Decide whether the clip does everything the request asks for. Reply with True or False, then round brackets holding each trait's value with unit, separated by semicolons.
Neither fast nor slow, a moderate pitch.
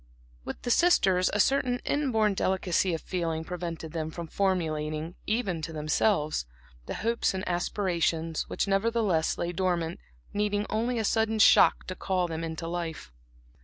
True (150 wpm; 180 Hz)